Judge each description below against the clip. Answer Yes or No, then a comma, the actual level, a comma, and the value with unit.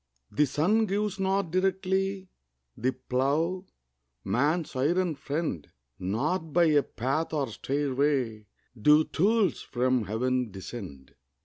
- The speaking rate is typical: No, slow, 110 wpm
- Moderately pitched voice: Yes, medium, 150 Hz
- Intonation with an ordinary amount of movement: No, wide, 6.4 semitones